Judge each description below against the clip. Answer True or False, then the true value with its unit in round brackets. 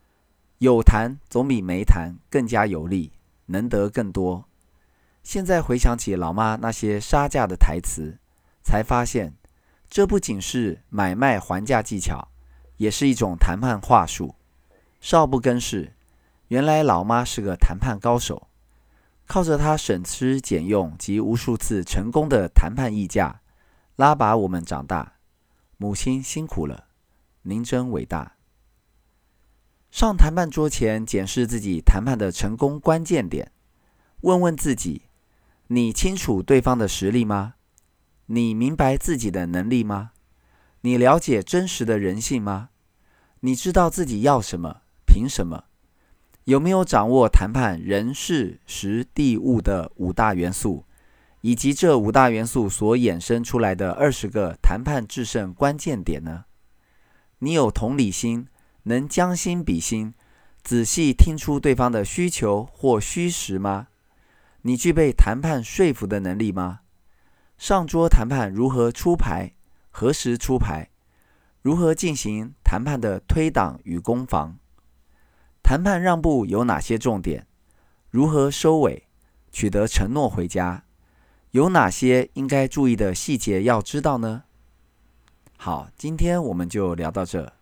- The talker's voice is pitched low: True (110 Hz)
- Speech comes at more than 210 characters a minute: False (205 characters per minute)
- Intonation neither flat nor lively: False (6.6 semitones)